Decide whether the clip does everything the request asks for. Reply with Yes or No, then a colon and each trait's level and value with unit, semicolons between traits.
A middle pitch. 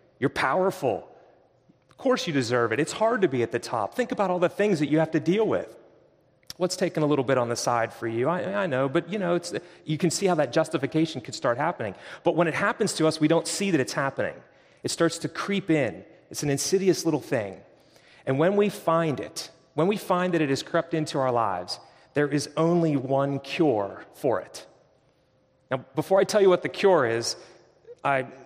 Yes: medium, 160 Hz